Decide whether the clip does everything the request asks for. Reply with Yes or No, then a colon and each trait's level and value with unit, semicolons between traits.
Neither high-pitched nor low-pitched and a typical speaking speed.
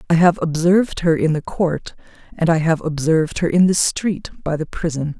No: medium, 165 Hz; fast, 210 wpm